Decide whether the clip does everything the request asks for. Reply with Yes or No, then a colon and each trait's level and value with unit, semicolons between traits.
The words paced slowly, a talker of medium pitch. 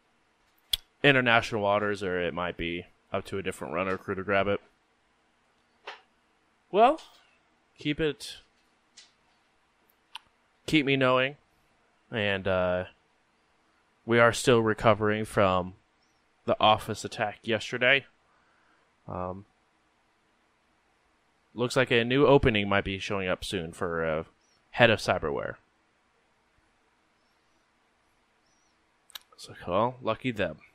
No: slow, 100 wpm; low, 100 Hz